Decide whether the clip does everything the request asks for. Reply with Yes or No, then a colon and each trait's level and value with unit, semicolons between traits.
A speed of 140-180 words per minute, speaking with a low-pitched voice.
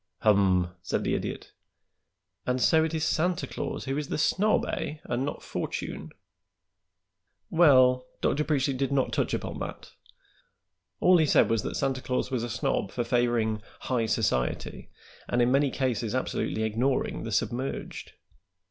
Yes: average, 155 wpm; low, 125 Hz